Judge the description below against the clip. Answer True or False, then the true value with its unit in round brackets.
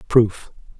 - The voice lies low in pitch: True (110 Hz)